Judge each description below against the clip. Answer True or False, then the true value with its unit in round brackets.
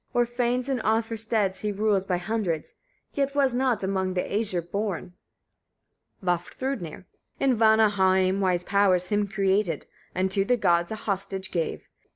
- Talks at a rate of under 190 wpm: True (155 wpm)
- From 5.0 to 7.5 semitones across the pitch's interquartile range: False (3.2 semitones)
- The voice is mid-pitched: False (200 Hz)